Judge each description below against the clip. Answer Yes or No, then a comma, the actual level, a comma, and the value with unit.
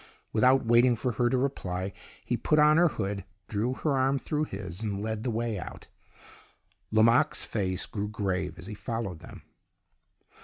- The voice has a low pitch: Yes, low, 110 Hz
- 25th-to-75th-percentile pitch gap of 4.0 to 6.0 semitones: Yes, average, 4.4 semitones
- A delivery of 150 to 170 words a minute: Yes, average, 165 wpm